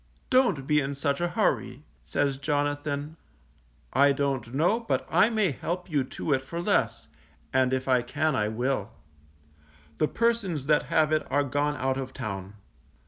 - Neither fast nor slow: Yes, average, 165 wpm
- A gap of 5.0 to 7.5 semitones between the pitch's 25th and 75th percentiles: No, average, 3.1 semitones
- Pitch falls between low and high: Yes, medium, 145 Hz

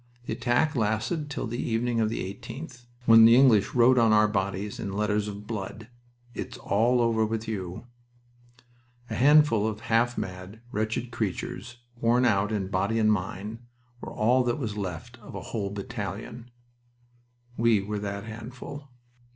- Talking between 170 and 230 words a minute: No, average, 160 wpm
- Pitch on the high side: No, low, 110 Hz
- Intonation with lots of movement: No, average, 2.8 semitones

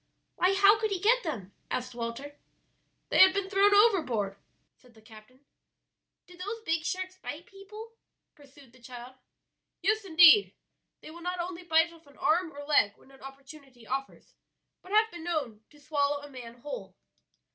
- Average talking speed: Yes, average, 170 wpm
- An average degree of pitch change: No, wide, 6.2 semitones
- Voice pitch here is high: Yes, very high, 315 Hz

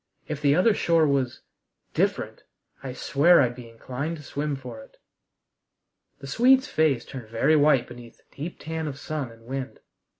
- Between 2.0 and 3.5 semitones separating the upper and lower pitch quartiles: No, average, 3.9 semitones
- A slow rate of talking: No, average, 170 wpm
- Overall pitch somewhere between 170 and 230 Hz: No, medium, 140 Hz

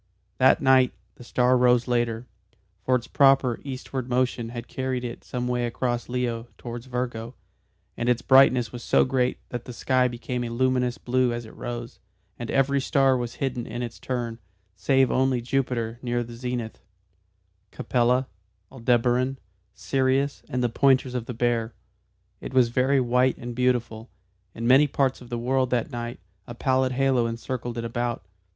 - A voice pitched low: Yes, low, 125 Hz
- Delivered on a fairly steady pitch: Yes, narrow, 1.5 semitones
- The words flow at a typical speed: Yes, average, 165 wpm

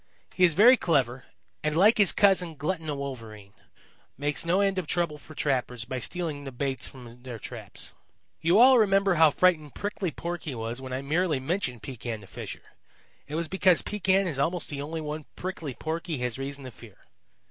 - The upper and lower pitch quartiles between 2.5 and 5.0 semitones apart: No, wide, 5.5 semitones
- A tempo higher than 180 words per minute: Yes, average, 190 wpm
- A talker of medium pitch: Yes, medium, 150 Hz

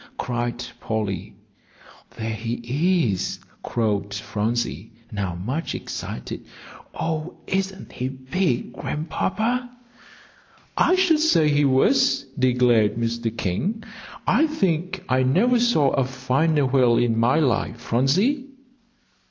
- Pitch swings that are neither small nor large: No, wide, 7.9 semitones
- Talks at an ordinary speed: No, slow, 110 wpm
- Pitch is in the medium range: No, low, 130 Hz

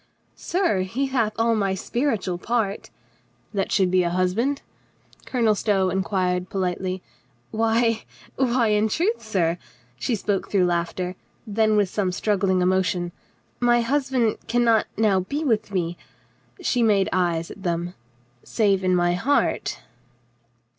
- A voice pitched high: Yes, high, 200 Hz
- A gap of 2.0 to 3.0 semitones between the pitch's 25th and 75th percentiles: No, average, 4.0 semitones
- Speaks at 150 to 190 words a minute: Yes, average, 160 wpm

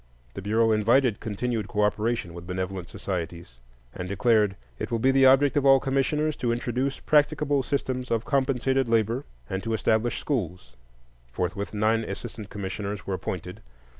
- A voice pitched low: Yes, low, 115 Hz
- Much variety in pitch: No, average, 5.0 semitones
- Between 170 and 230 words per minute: No, average, 150 wpm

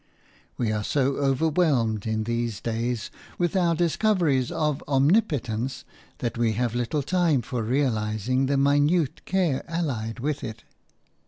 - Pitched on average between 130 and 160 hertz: Yes, low, 135 Hz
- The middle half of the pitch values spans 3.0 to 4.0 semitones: No, average, 4.8 semitones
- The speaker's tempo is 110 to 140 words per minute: Yes, slow, 135 wpm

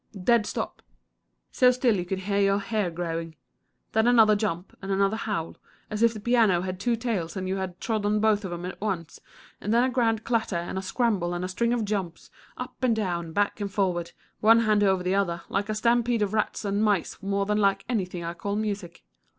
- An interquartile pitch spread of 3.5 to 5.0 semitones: No, average, 3.1 semitones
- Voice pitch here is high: Yes, high, 200 Hz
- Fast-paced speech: Yes, fast, 215 wpm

